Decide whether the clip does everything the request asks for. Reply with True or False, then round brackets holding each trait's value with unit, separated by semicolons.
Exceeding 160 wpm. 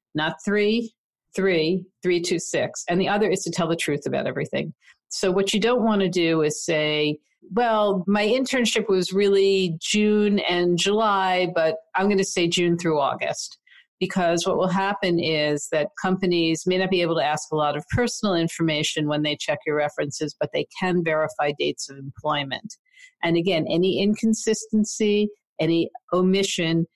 True (170 wpm)